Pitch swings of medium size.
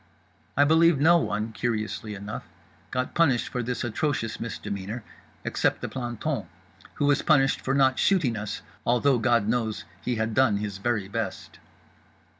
Yes: average, 3.9 semitones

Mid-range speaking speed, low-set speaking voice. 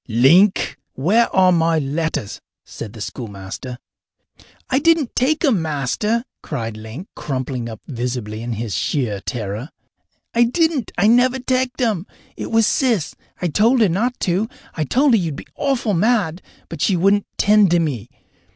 No: average, 160 wpm; medium, 175 Hz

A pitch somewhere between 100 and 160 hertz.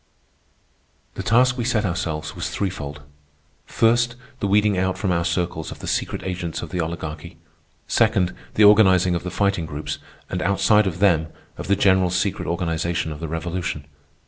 No: very low, 90 Hz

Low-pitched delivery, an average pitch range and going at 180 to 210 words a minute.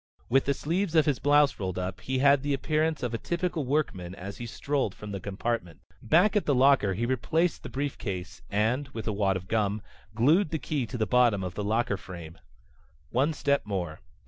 No: low, 120 Hz; wide, 6.4 semitones; fast, 205 wpm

